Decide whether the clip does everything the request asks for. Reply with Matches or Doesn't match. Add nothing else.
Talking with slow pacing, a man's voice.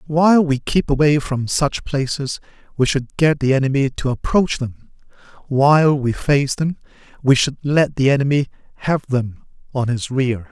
Doesn't match